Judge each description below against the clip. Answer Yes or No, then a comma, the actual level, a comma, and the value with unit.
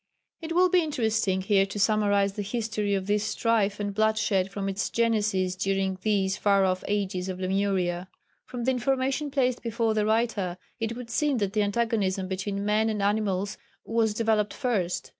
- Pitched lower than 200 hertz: No, high, 210 Hz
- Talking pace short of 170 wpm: No, average, 175 wpm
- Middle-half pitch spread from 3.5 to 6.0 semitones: No, average, 2.8 semitones